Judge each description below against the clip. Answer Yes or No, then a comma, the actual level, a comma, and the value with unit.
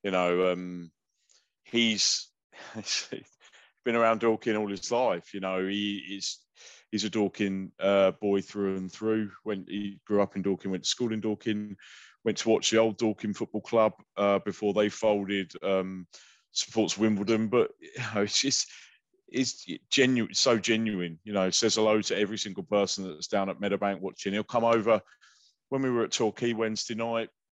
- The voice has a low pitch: Yes, low, 105 Hz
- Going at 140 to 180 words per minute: Yes, average, 175 wpm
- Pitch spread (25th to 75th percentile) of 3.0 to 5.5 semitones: No, narrow, 2.4 semitones